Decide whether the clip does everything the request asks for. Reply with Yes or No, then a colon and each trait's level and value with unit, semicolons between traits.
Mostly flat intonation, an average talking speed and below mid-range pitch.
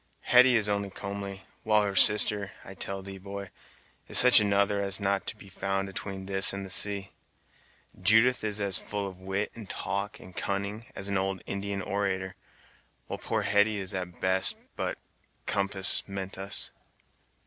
Yes: narrow, 0.9 semitones; average, 175 wpm; low, 100 Hz